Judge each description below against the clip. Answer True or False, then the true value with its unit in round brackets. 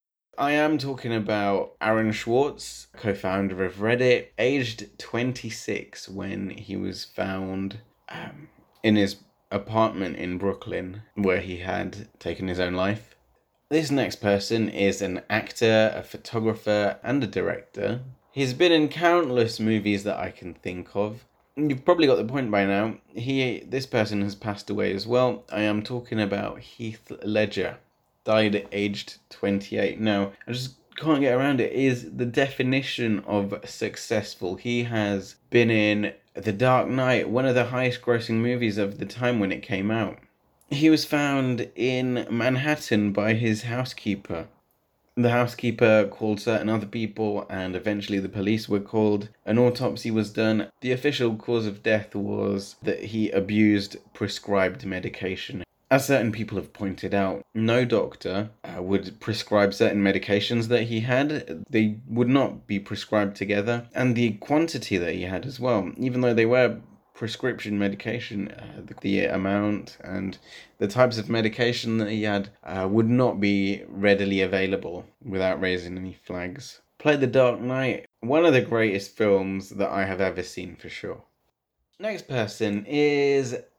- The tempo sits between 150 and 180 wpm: True (155 wpm)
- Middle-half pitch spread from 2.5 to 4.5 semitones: True (3.6 semitones)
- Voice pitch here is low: True (110 Hz)